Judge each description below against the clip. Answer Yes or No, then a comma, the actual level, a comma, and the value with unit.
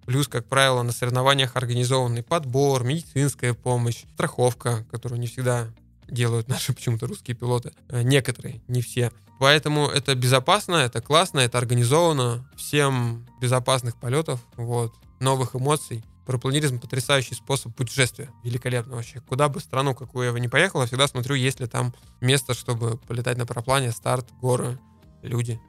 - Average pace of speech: Yes, average, 145 wpm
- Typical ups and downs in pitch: No, narrow, 2.1 semitones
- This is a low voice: Yes, low, 125 Hz